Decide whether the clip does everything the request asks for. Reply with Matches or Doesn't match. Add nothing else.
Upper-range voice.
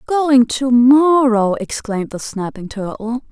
Matches